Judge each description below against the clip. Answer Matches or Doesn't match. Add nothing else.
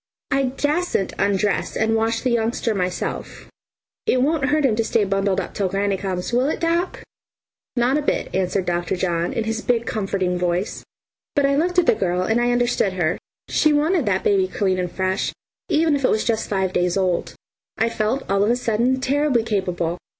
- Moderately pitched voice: Doesn't match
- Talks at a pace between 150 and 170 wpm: Doesn't match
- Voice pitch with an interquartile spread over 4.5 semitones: Matches